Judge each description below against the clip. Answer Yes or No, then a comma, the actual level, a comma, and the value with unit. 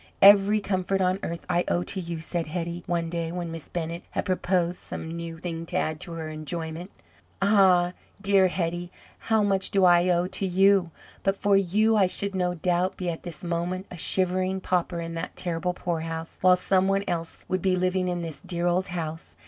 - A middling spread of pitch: No, narrow, 1.9 semitones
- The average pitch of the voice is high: No, medium, 180 Hz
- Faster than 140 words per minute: Yes, average, 200 wpm